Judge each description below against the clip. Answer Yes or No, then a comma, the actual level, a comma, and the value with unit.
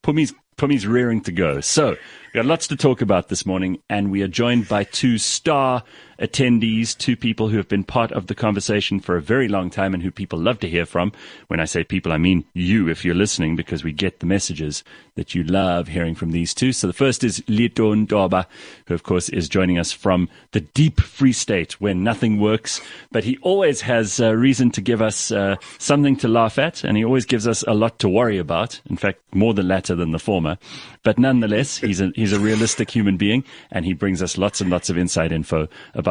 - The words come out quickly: Yes, fast, 230 wpm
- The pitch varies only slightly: No, average, 4.5 semitones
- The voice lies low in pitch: Yes, low, 105 Hz